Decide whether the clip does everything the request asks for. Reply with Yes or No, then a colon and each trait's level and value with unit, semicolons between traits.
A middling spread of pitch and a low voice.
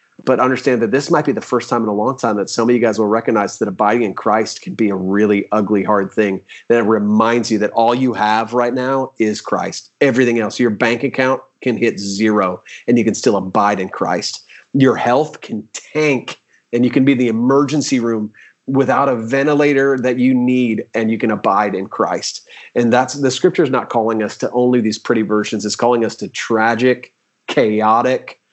Yes: average, 3.0 semitones; low, 120 Hz